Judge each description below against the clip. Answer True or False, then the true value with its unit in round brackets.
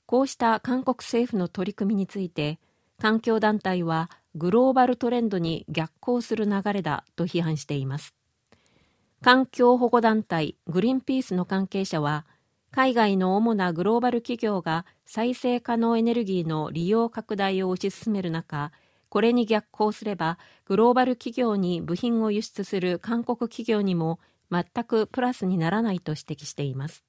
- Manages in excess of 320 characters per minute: False (255 characters per minute)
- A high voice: True (205 Hz)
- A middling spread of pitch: False (5.7 semitones)